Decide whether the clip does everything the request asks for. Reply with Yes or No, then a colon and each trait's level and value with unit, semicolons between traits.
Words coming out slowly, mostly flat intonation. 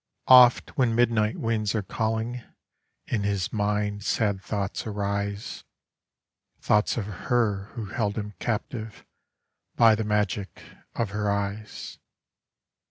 Yes: slow, 115 wpm; narrow, 1.8 semitones